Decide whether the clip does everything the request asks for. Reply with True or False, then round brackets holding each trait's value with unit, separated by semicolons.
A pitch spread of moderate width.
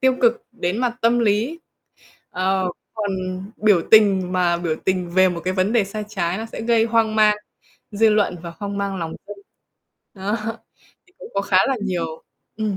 True (3.2 semitones)